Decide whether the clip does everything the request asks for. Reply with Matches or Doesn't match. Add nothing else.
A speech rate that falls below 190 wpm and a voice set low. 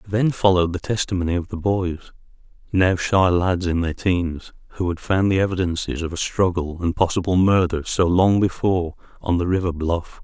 Matches